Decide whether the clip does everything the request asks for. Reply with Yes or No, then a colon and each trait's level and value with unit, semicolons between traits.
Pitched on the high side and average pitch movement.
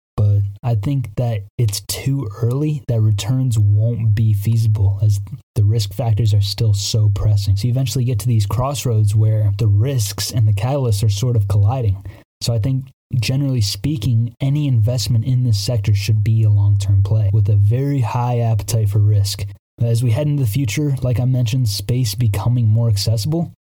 No: low, 115 Hz; average, 3.1 semitones